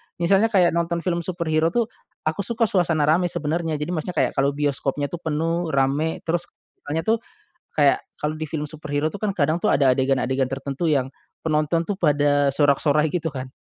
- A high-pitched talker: No, medium, 155 Hz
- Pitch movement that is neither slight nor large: Yes, average, 3.0 semitones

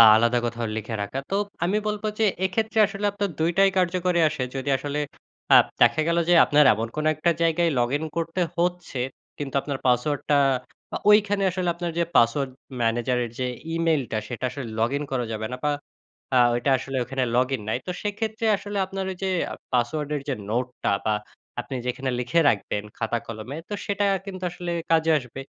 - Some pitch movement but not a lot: No, wide, 6.4 semitones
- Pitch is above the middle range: No, medium, 145 Hz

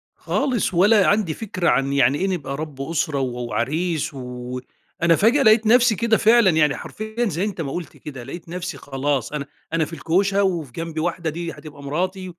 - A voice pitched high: No, medium, 165 Hz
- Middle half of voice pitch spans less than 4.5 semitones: No, wide, 5.6 semitones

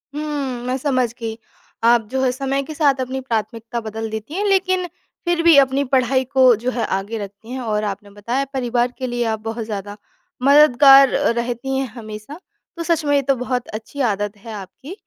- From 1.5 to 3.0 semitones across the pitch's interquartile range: No, average, 3.7 semitones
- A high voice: Yes, very high, 250 Hz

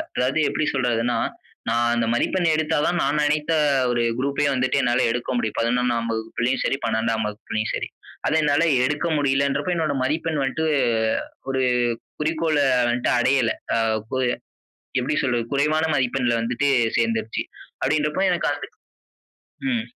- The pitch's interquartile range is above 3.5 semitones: Yes, average, 4.2 semitones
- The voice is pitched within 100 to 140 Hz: Yes, low, 135 Hz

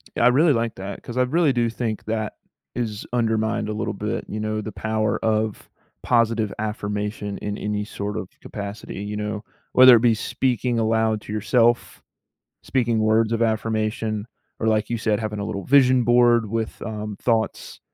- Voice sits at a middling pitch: No, low, 110 Hz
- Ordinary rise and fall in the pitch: No, narrow, 1.8 semitones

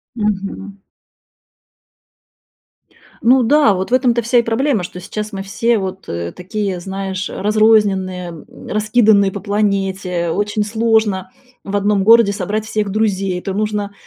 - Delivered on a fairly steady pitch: Yes, narrow, 2.3 semitones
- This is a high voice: Yes, high, 205 Hz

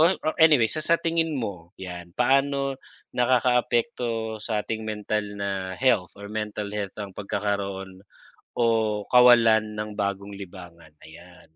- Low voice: Yes, low, 105 Hz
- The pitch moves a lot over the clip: No, average, 4.0 semitones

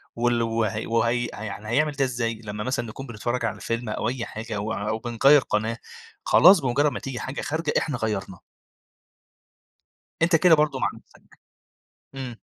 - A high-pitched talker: No, low, 120 Hz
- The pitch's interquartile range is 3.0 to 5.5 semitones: Yes, average, 3.5 semitones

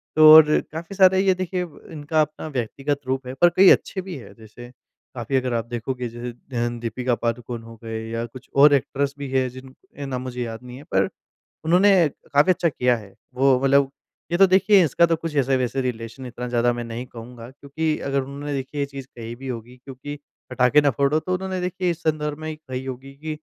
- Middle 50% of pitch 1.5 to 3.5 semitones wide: No, average, 4.1 semitones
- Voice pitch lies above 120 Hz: Yes, low, 135 Hz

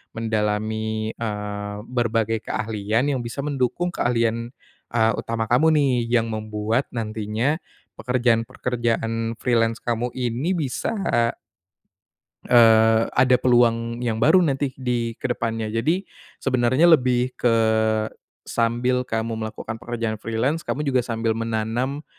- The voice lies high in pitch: No, low, 115 Hz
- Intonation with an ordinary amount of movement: No, narrow, 2.1 semitones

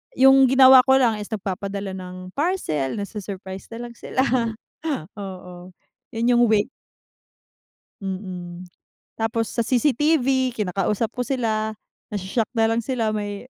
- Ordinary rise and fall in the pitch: Yes, average, 4.5 semitones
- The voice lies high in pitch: Yes, high, 220 Hz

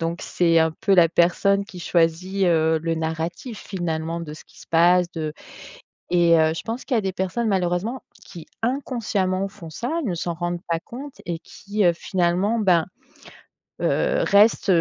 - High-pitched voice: No, medium, 175 Hz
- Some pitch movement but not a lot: Yes, average, 3.2 semitones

